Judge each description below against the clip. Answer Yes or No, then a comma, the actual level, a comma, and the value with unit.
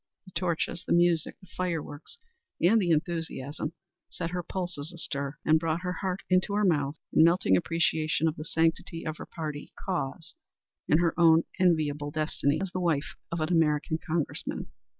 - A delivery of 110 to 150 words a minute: No, average, 170 wpm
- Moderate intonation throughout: No, narrow, 2.3 semitones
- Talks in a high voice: No, medium, 165 Hz